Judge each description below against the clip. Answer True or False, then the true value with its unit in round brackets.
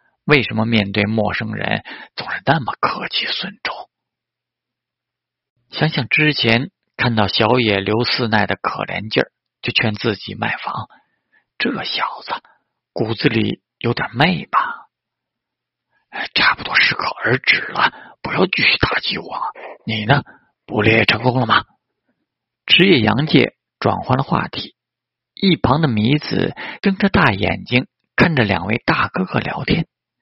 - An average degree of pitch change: True (5.0 semitones)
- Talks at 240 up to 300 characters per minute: False (200 characters per minute)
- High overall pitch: False (115 Hz)